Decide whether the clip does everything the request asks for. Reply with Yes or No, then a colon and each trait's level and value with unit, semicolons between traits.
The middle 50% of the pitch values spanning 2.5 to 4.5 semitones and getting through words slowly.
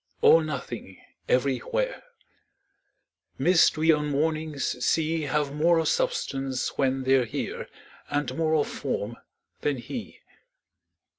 Yes: average, 3.3 semitones; slow, 115 wpm